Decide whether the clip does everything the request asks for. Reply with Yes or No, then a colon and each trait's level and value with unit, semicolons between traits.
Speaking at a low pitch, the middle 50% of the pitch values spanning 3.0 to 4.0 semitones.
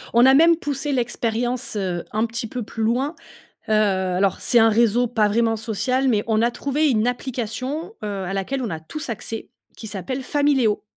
No: high, 235 Hz; average, 3.6 semitones